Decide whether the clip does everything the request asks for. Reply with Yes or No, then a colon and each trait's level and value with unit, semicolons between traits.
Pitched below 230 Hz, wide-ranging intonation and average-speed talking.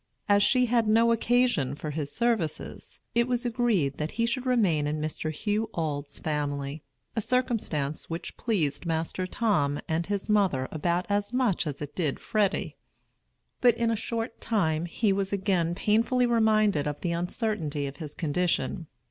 Yes: high, 190 Hz; wide, 6.8 semitones; average, 165 wpm